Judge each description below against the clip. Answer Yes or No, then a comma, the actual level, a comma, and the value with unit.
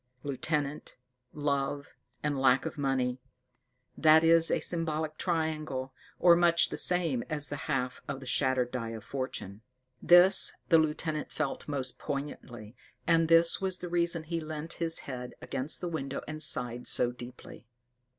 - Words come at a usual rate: Yes, average, 150 wpm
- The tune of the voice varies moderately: Yes, average, 3.9 semitones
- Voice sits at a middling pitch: Yes, medium, 150 Hz